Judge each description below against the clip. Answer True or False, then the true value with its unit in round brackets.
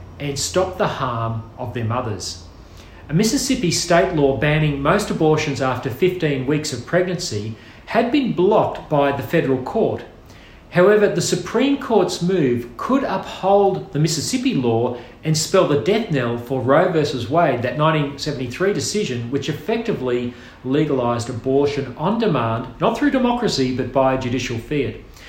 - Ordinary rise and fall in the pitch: False (6.7 semitones)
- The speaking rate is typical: True (145 wpm)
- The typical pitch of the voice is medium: True (145 Hz)